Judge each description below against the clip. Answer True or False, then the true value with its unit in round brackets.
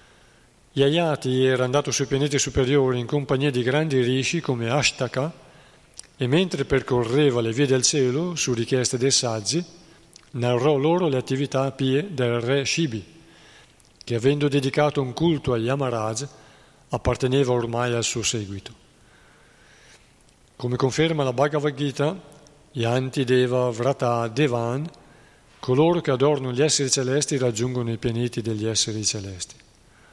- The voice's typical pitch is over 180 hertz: False (135 Hz)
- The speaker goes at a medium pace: True (130 wpm)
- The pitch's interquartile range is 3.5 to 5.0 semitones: False (3.0 semitones)